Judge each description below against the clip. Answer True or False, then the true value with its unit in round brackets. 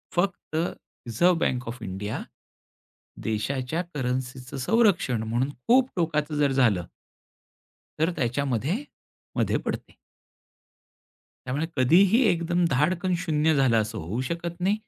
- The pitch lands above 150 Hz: False (140 Hz)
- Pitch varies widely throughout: True (5.8 semitones)